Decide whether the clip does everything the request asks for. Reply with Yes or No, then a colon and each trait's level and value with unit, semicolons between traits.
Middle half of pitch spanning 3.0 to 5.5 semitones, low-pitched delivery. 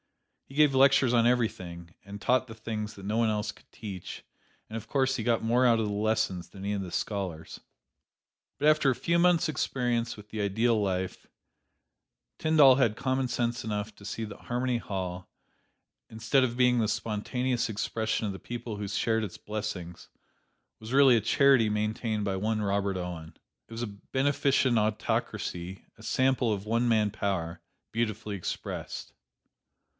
Yes: average, 3.3 semitones; low, 110 Hz